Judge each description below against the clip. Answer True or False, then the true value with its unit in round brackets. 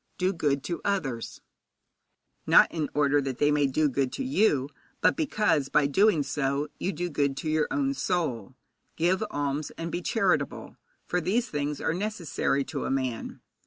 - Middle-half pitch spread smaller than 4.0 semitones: False (4.7 semitones)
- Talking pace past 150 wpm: True (170 wpm)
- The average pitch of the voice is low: False (150 Hz)